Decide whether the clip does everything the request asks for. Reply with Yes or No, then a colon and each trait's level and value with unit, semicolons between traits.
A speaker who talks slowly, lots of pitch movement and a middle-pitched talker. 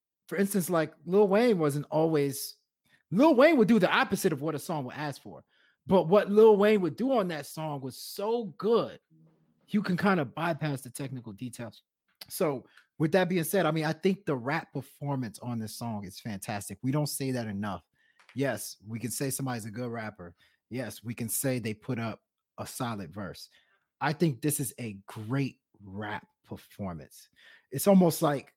No: average, 190 wpm; wide, 7.2 semitones; medium, 145 Hz